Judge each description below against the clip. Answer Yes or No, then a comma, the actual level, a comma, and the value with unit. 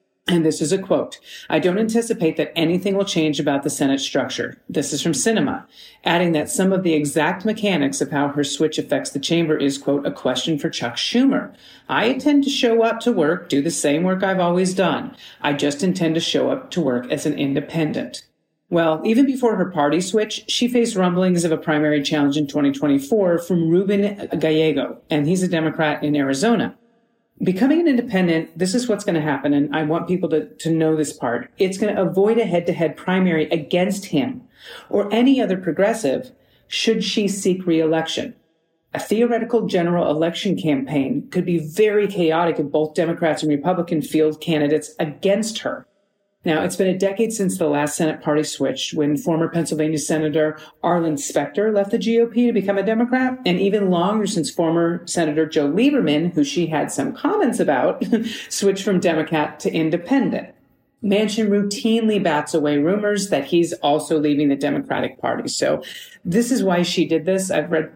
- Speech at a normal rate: Yes, average, 185 wpm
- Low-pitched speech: No, medium, 170 Hz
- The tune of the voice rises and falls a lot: No, average, 5.0 semitones